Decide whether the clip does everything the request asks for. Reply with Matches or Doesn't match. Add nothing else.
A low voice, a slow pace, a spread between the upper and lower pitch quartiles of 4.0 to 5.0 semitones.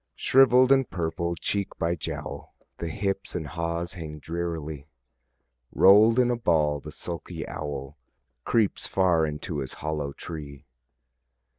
Matches